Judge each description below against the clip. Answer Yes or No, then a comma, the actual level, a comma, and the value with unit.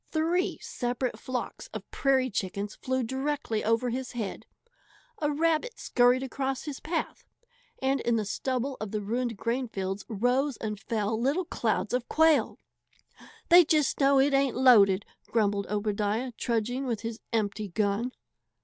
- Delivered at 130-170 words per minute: Yes, average, 145 wpm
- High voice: Yes, high, 245 Hz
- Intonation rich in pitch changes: No, average, 4.1 semitones